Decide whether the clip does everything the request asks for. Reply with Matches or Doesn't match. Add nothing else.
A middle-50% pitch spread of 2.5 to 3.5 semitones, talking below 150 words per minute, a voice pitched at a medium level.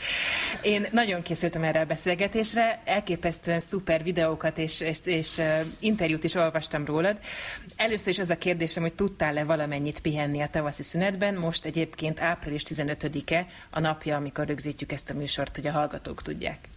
Doesn't match